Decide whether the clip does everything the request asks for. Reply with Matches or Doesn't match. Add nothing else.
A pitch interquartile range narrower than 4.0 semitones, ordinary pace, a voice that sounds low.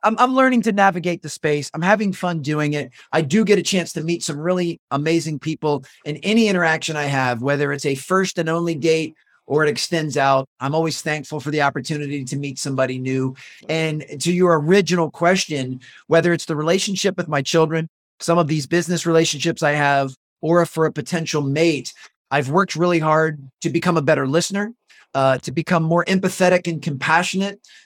Doesn't match